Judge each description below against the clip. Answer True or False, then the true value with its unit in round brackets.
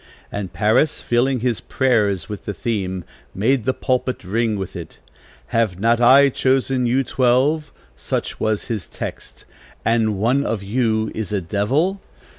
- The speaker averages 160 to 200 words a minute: False (150 wpm)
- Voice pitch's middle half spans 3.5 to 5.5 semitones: True (4.2 semitones)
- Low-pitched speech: True (115 Hz)